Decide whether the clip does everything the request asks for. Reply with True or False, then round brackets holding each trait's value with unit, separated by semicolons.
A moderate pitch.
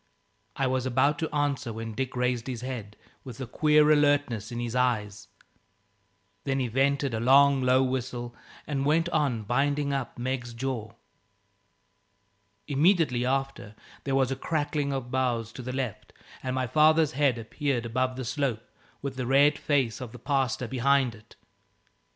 False (130 Hz)